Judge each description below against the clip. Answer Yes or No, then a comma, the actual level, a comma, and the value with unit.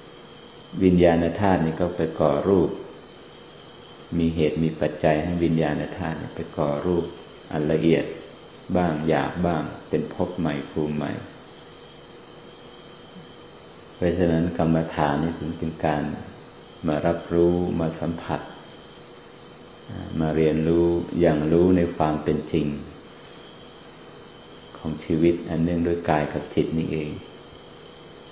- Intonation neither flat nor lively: No, narrow, 1.8 semitones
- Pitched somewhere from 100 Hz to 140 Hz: No, very low, 80 Hz